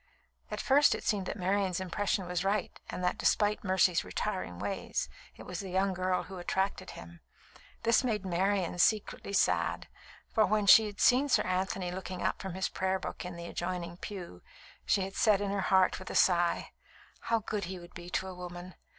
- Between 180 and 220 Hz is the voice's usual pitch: Yes, high, 190 Hz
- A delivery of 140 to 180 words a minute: No, average, 195 wpm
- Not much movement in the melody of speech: Yes, narrow, 2.1 semitones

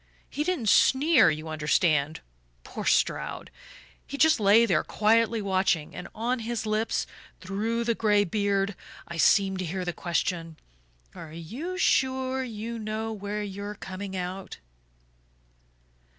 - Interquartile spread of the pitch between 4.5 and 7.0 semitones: No, average, 3.9 semitones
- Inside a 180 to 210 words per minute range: No, slow, 135 wpm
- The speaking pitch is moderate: No, high, 205 Hz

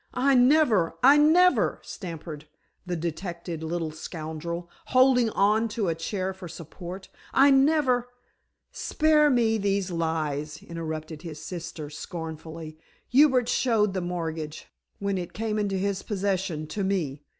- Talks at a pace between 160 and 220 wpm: No, slow, 135 wpm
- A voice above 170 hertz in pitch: Yes, medium, 185 Hz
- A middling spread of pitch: No, wide, 5.8 semitones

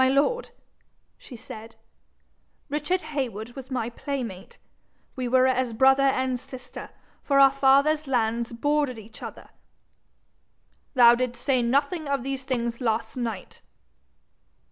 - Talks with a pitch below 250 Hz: No, very high, 260 Hz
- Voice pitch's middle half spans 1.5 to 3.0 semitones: Yes, average, 2.7 semitones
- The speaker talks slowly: Yes, slow, 120 wpm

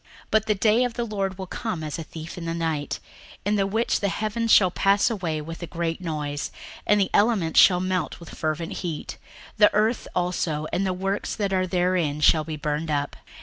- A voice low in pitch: No, medium, 180 Hz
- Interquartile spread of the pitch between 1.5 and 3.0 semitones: No, average, 4.1 semitones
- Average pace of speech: No, fast, 215 wpm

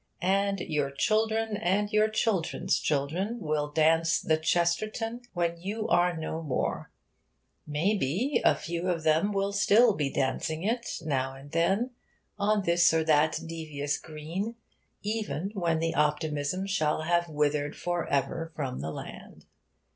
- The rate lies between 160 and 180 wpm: No, average, 140 wpm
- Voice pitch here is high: No, medium, 170 Hz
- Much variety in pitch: No, average, 5.0 semitones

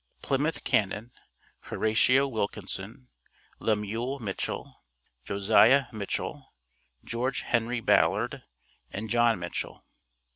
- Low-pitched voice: Yes, low, 115 Hz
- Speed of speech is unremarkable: No, slow, 80 wpm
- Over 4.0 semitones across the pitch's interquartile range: No, average, 3.2 semitones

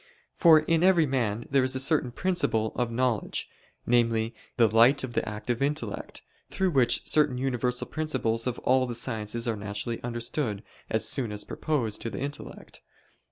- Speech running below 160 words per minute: No, average, 165 wpm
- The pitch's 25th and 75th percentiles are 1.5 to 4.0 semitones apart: Yes, average, 3.5 semitones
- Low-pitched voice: Yes, low, 125 Hz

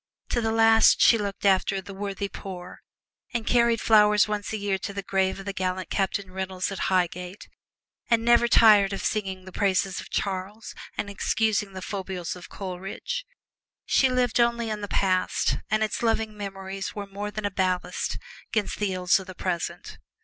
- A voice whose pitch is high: Yes, high, 200 Hz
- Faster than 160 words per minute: Yes, average, 180 wpm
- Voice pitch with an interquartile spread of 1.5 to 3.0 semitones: Yes, narrow, 2.4 semitones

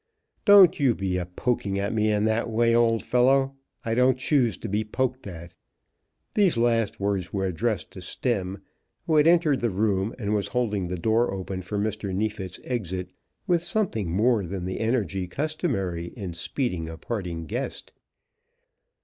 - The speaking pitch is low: Yes, low, 110 Hz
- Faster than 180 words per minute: No, average, 165 wpm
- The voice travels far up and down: No, average, 4.6 semitones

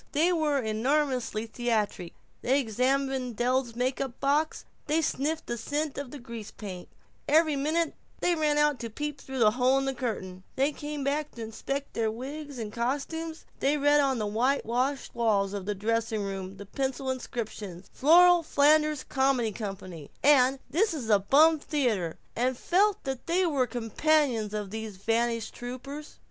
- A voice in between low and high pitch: No, very high, 260 Hz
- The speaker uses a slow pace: No, average, 165 wpm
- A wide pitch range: No, average, 4.7 semitones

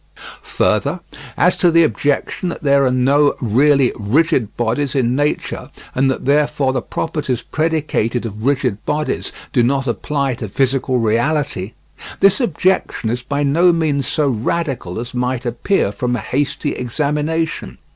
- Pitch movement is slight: No, average, 3.6 semitones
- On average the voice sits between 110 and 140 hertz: Yes, low, 135 Hz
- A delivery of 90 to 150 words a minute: Yes, average, 145 wpm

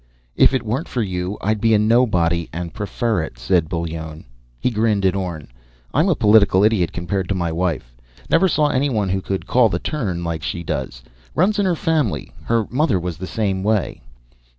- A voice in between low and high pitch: No, low, 100 Hz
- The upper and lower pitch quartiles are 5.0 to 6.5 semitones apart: Yes, average, 5.3 semitones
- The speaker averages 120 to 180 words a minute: No, average, 195 wpm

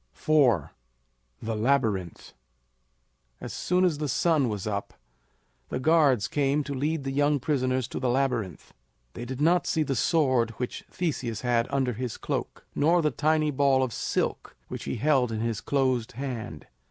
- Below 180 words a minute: Yes, average, 165 wpm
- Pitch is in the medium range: No, low, 130 Hz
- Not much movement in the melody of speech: No, average, 4.0 semitones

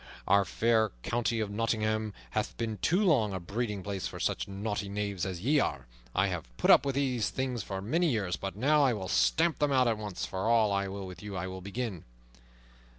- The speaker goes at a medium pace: No, fast, 210 wpm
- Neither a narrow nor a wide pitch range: Yes, average, 3.8 semitones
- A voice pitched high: No, low, 105 Hz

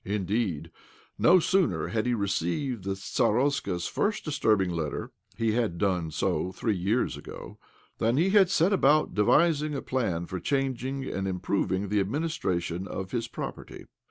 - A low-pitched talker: Yes, low, 110 Hz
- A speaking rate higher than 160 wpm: No, average, 155 wpm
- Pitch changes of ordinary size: No, wide, 6.7 semitones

